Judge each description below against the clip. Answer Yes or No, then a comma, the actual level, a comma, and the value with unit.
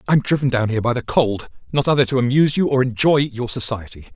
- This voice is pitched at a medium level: No, low, 125 Hz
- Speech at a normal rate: No, fast, 230 wpm